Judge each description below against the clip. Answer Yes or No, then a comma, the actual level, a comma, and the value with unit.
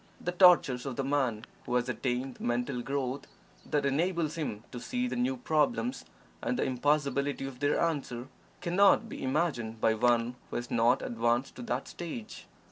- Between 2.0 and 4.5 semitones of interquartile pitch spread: No, average, 4.9 semitones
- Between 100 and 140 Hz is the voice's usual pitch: Yes, low, 135 Hz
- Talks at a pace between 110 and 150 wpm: No, average, 175 wpm